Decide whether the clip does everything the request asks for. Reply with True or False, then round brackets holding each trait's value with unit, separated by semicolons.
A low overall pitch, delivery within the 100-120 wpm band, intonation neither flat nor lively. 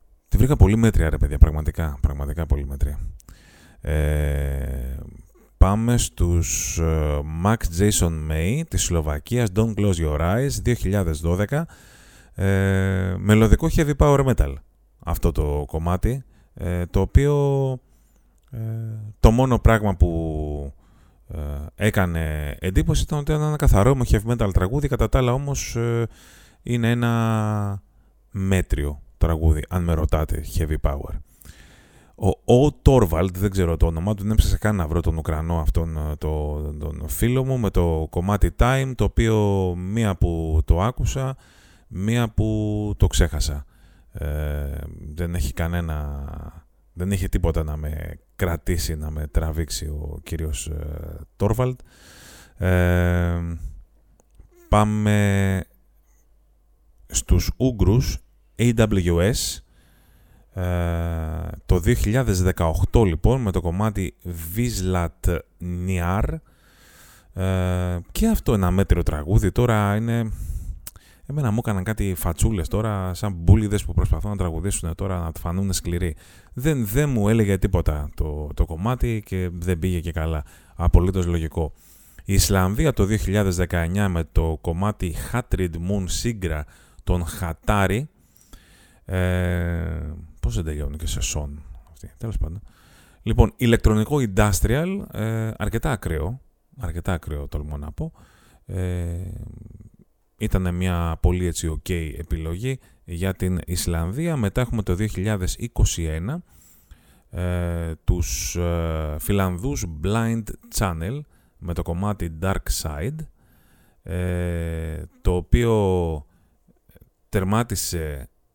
True (90 Hz; 115 wpm; 4.9 semitones)